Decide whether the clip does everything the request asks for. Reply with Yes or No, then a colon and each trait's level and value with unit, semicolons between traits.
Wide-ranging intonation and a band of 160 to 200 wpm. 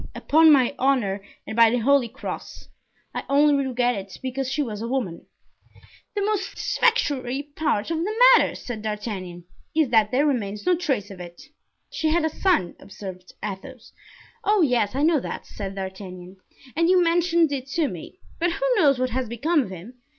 Yes: wide, 7.1 semitones; average, 180 wpm